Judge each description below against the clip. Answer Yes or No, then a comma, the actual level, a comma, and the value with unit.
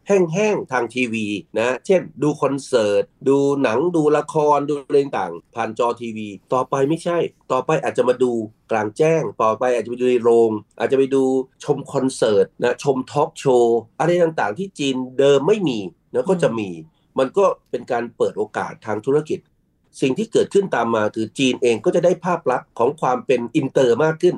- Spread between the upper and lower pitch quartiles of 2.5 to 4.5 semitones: No, wide, 5.5 semitones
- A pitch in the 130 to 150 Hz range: Yes, low, 135 Hz